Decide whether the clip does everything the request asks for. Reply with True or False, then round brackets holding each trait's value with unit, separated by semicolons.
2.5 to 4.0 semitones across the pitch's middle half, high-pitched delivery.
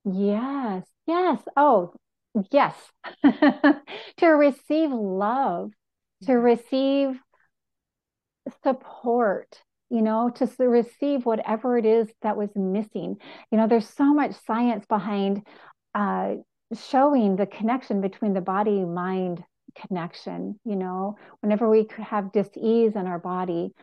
False (4.7 semitones; 225 Hz)